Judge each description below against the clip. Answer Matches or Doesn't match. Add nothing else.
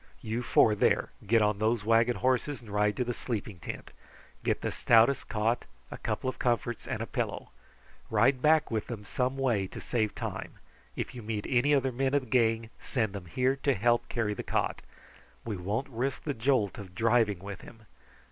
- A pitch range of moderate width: Matches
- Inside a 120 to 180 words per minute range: Doesn't match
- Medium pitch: Doesn't match